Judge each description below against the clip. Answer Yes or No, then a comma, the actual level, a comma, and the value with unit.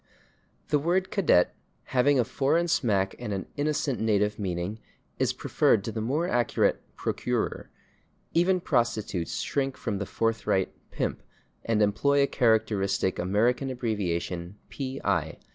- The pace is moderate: No, slow, 130 wpm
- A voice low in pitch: Yes, low, 115 Hz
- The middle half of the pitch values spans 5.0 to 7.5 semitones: Yes, wide, 5.6 semitones